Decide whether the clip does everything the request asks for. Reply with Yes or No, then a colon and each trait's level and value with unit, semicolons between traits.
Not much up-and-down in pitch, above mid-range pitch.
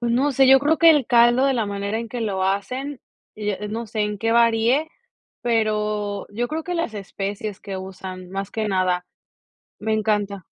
No: average, 3.3 semitones; high, 215 Hz